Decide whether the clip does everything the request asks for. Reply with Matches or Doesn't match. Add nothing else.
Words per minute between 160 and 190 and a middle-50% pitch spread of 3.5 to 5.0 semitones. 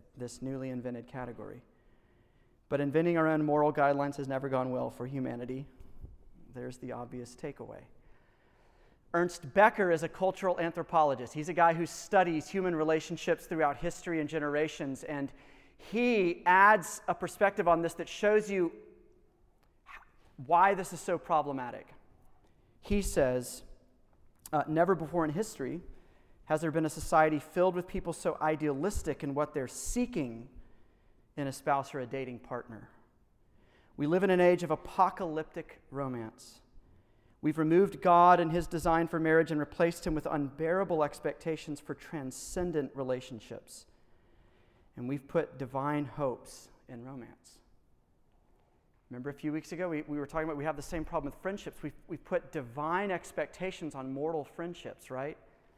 Doesn't match